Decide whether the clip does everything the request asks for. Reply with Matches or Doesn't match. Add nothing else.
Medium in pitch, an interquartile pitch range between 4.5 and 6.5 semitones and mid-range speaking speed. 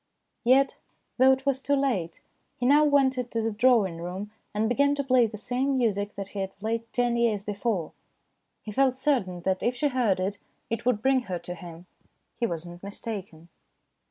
Doesn't match